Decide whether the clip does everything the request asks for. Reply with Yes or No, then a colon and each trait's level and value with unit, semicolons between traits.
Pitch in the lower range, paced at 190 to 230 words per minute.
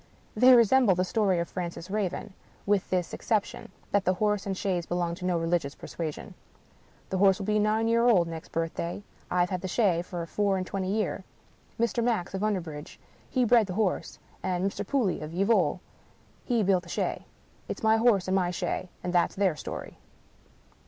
No: high, 190 Hz; average, 200 wpm